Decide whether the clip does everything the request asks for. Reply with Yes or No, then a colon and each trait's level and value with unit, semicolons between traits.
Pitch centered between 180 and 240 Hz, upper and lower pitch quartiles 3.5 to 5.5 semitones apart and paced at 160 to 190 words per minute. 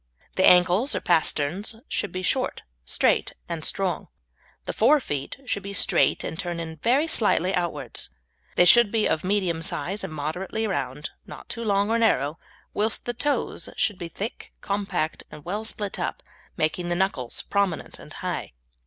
Yes: medium, 185 Hz; average, 4.3 semitones; average, 165 wpm